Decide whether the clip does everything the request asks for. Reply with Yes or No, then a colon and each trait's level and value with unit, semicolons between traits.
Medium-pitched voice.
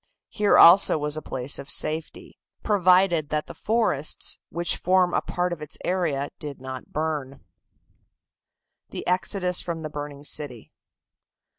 Yes: medium, 155 Hz